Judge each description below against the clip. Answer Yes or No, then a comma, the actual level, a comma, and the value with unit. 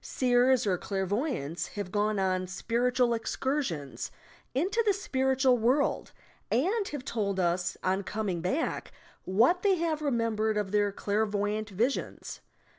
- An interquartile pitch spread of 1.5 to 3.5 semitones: No, average, 5.3 semitones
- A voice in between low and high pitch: No, high, 220 Hz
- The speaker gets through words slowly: Yes, slow, 130 wpm